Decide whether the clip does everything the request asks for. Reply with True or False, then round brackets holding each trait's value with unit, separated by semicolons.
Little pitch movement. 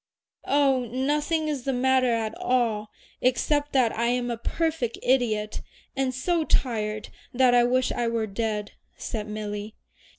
False (3.2 semitones)